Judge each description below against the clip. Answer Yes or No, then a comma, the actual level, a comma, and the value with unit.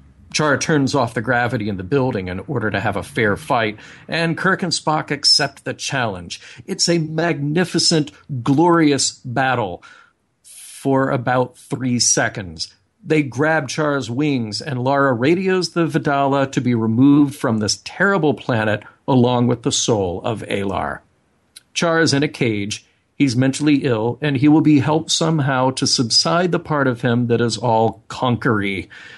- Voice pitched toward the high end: No, low, 135 Hz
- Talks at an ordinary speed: Yes, average, 160 wpm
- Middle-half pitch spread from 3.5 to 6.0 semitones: Yes, average, 4.3 semitones